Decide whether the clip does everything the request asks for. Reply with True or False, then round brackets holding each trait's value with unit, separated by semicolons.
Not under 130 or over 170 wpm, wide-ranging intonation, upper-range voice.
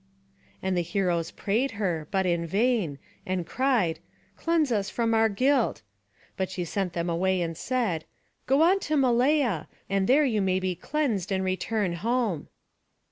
True (160 wpm; 5.9 semitones; 195 Hz)